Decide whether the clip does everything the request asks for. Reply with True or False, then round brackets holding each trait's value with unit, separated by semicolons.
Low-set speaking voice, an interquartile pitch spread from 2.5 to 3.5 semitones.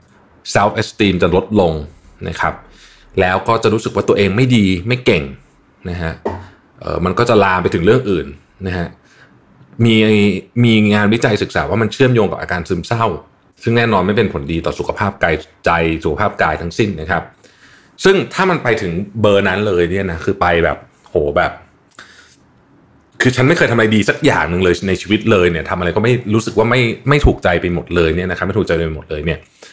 False (100 Hz; 4.4 semitones)